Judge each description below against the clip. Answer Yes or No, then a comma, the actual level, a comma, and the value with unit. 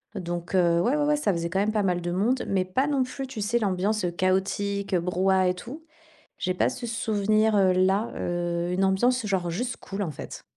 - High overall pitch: Yes, high, 195 Hz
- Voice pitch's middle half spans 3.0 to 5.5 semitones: Yes, average, 3.4 semitones